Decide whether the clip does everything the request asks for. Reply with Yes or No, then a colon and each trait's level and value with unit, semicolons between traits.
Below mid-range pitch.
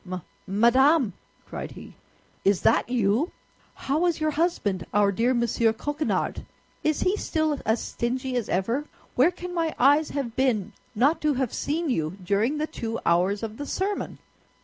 No: very high, 255 Hz